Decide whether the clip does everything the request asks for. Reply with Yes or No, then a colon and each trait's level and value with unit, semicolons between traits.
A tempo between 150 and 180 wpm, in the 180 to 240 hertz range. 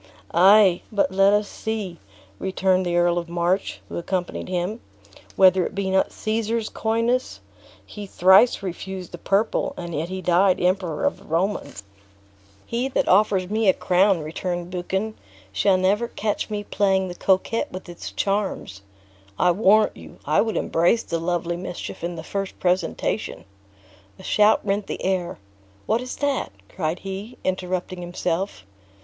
Yes: average, 155 wpm; high, 190 Hz